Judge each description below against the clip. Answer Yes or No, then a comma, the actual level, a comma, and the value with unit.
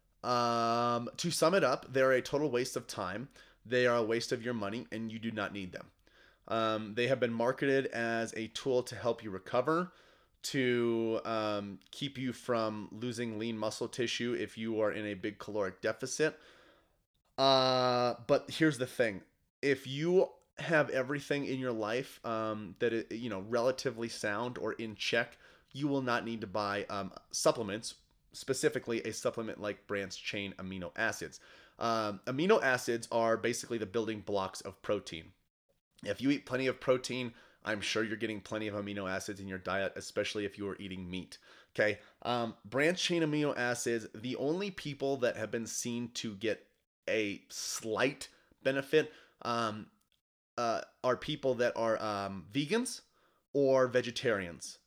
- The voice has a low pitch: Yes, low, 115 Hz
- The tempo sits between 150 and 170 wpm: Yes, average, 165 wpm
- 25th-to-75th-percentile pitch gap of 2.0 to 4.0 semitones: Yes, average, 3.5 semitones